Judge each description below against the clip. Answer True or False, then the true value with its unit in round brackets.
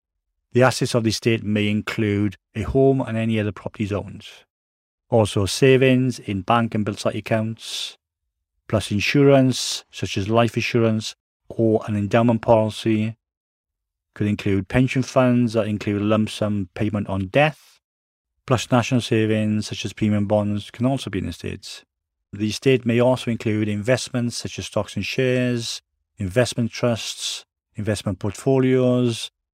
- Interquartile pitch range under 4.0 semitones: True (3.3 semitones)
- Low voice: True (110 Hz)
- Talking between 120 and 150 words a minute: True (145 wpm)